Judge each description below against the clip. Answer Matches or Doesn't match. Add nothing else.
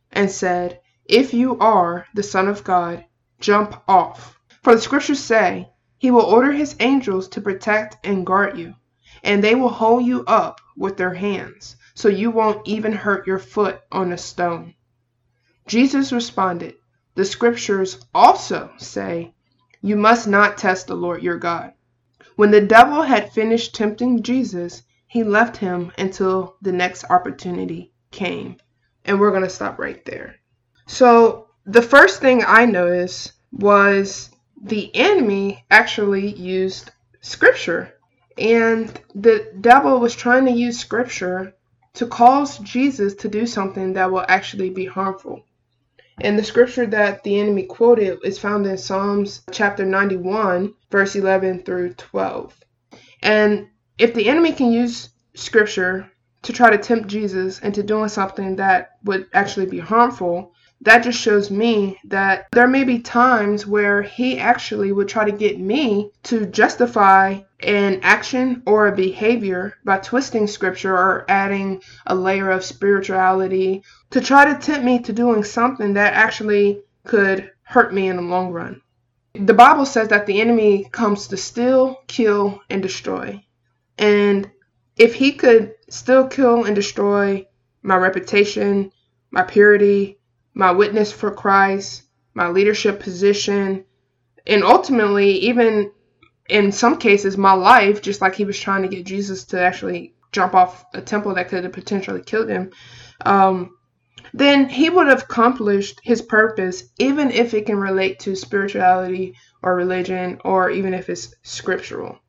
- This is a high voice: Matches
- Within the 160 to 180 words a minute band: Doesn't match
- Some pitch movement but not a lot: Matches